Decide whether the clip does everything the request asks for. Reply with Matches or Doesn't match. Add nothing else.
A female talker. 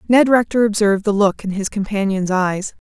Matches